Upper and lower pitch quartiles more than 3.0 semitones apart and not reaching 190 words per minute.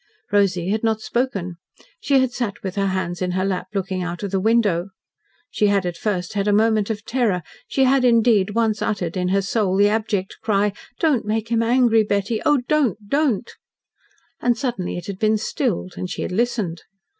No: average, 3.5 semitones; average, 195 wpm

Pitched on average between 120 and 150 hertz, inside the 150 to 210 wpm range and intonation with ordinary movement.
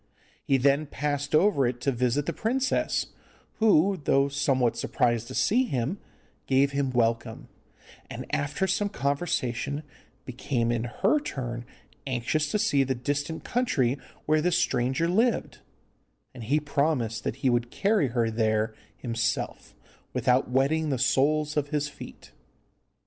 No: medium, 140 Hz; average, 140 wpm; average, 4.0 semitones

